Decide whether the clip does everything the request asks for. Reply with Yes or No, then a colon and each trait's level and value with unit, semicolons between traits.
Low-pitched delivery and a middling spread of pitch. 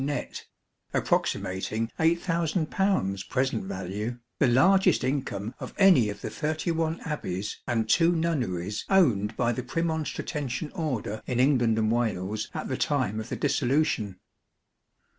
No: low, 125 Hz; wide, 6.6 semitones